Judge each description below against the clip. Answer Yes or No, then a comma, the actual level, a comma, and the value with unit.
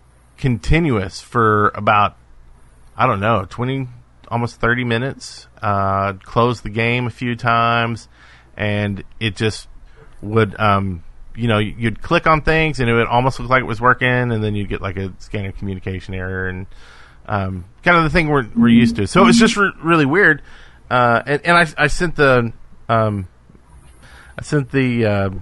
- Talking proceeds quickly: No, average, 175 wpm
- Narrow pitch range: No, average, 4.5 semitones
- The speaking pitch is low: Yes, low, 115 Hz